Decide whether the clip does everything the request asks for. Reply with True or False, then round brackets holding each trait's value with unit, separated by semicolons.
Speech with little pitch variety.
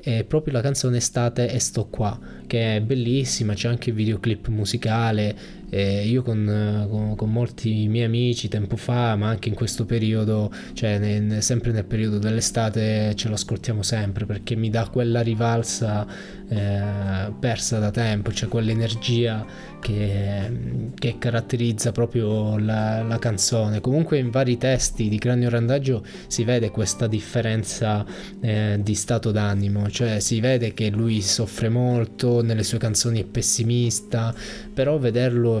True (2.0 semitones)